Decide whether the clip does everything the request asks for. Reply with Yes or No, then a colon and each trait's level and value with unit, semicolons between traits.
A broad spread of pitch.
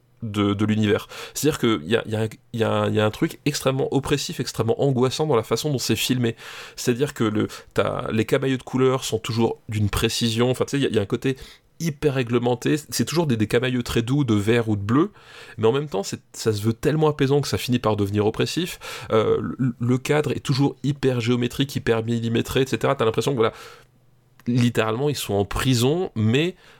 No: average, 3.5 semitones